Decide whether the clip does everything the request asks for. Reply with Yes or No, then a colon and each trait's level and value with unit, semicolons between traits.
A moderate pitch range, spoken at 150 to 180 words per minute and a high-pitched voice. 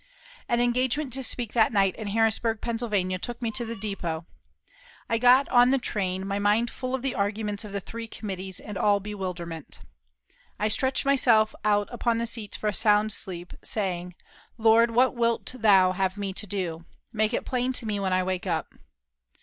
No: average, 3.5 semitones; average, 190 wpm; high, 215 Hz